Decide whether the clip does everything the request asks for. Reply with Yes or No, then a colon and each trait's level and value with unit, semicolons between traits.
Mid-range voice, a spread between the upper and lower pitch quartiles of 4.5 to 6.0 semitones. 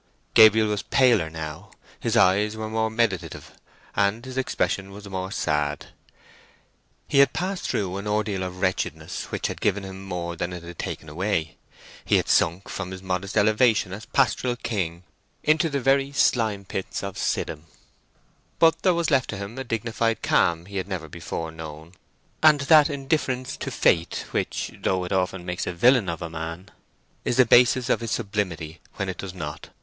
No: low, 100 Hz; average, 5.2 semitones